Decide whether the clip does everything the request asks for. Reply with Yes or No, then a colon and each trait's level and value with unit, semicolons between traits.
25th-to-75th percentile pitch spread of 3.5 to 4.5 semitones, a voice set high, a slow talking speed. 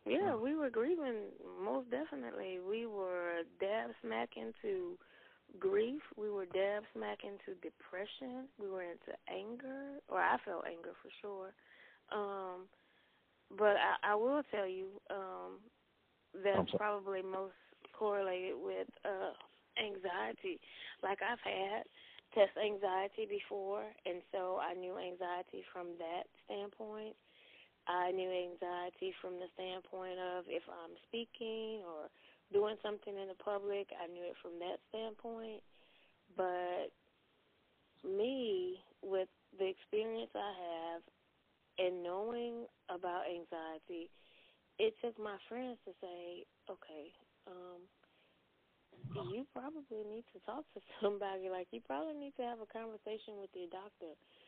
Yes: average, 4.0 semitones; high, 200 Hz; slow, 130 wpm